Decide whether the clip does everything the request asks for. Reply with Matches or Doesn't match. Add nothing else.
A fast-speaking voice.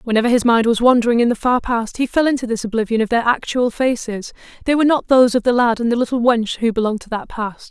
Matches